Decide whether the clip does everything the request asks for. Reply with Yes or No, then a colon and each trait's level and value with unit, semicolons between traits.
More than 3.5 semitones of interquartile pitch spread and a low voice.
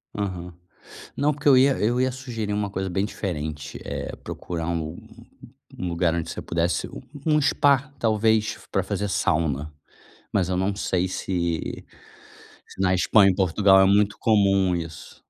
Yes: average, 3.9 semitones; very low, 95 Hz